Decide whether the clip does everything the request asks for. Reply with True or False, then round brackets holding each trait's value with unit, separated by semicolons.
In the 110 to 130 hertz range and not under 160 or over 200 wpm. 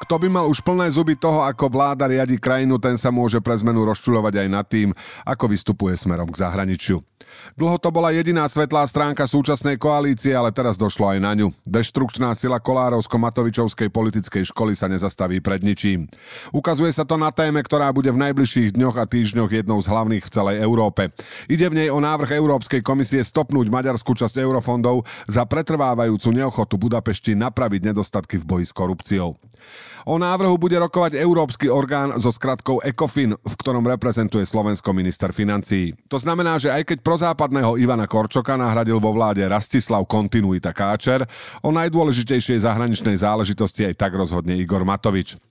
True (120 Hz; 165 wpm)